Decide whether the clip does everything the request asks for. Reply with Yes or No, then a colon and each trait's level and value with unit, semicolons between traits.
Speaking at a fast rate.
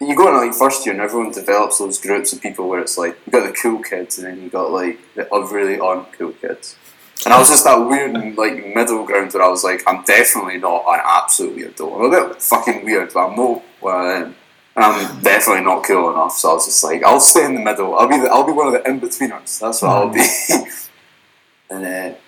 Yes: fast, 255 wpm